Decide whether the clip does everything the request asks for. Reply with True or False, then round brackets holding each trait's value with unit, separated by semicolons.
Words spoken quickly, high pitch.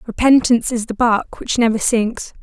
False (175 wpm; 230 Hz)